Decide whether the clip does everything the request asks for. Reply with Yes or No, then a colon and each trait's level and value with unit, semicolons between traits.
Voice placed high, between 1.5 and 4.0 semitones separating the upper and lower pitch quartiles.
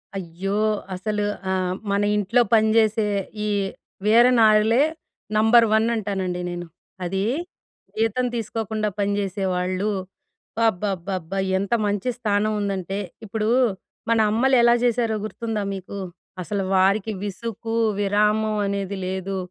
Yes: high, 205 Hz; narrow, 2.4 semitones